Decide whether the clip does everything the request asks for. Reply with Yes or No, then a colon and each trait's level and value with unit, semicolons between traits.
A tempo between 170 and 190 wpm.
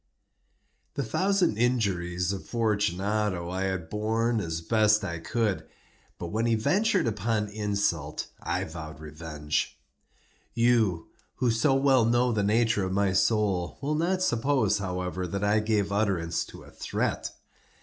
No: average, 140 wpm